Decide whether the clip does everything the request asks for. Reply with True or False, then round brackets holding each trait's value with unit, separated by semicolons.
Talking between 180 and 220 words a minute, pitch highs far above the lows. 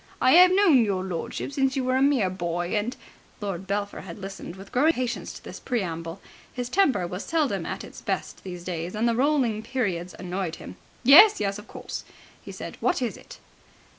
True (200 wpm; 6.2 semitones)